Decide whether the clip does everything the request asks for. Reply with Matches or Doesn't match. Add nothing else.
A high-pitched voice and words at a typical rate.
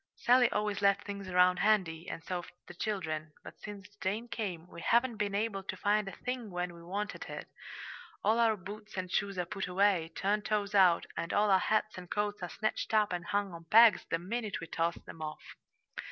Doesn't match